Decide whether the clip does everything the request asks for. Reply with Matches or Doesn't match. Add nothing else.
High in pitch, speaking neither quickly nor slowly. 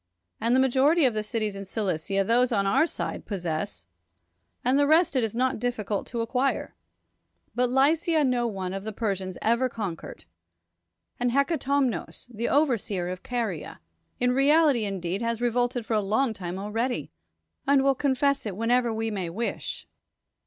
Matches